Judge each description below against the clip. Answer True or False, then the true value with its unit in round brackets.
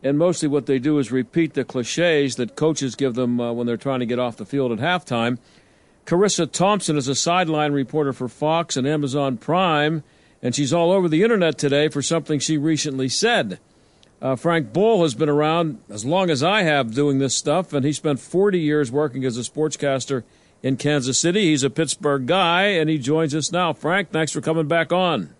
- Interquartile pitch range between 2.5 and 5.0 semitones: True (3.5 semitones)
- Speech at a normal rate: False (210 wpm)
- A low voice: False (150 Hz)